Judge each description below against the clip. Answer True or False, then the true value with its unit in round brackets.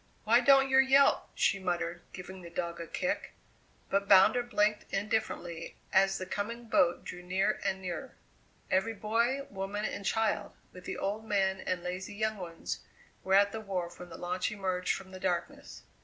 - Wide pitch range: False (3.1 semitones)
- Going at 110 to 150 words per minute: False (175 wpm)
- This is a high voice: True (195 Hz)